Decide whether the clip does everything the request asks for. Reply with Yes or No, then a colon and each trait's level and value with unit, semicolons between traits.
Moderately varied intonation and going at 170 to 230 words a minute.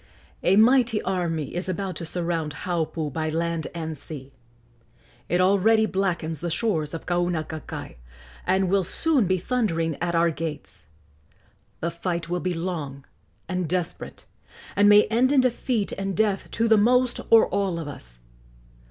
No: average, 3.9 semitones; average, 150 wpm